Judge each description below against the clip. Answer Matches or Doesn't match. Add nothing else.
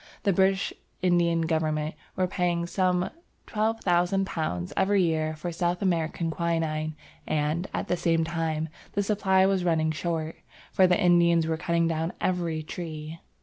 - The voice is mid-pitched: Matches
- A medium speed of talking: Matches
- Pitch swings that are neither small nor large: Doesn't match